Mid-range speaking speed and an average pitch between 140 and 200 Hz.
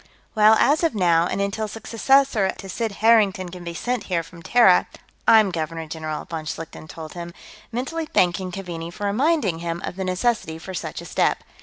Yes: average, 190 wpm; high, 190 Hz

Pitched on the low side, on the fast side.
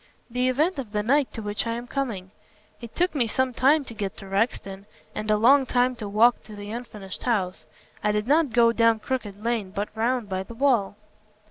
No: high, 230 Hz; fast, 215 wpm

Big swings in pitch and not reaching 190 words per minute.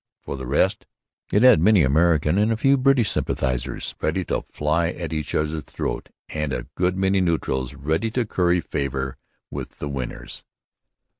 Yes: wide, 5.8 semitones; average, 165 wpm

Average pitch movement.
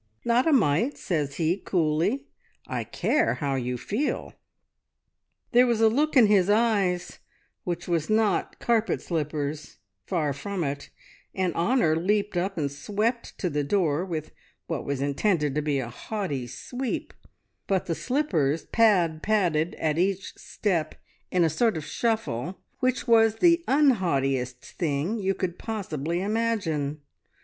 No: wide, 6.5 semitones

